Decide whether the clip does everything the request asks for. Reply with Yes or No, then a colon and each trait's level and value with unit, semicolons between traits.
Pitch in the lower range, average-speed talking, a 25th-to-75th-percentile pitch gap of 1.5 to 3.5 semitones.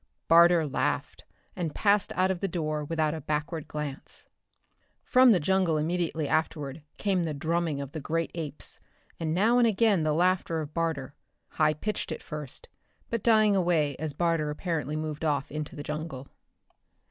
No: medium, 160 Hz; average, 165 wpm; average, 2.9 semitones